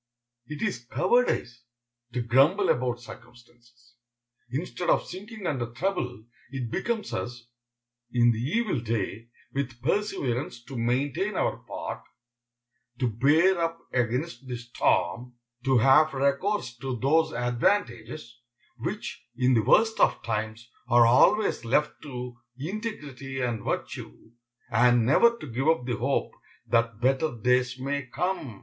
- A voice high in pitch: No, low, 130 Hz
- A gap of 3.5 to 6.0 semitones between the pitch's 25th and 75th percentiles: Yes, average, 4.7 semitones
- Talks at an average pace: No, slow, 130 wpm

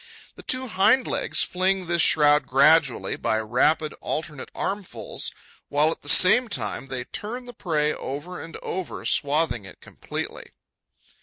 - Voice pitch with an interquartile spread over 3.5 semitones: Yes, average, 5.0 semitones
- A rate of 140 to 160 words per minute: Yes, average, 145 wpm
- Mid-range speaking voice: Yes, medium, 160 Hz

